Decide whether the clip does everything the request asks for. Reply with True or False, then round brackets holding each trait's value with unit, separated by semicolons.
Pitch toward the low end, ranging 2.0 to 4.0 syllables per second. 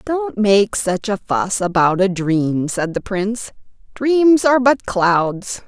False (205 Hz; 3.5 syllables/s)